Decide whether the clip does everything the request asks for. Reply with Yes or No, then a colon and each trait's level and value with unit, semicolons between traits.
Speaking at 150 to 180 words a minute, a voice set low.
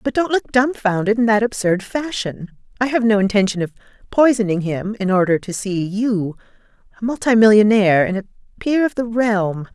No: average, 170 wpm; high, 215 Hz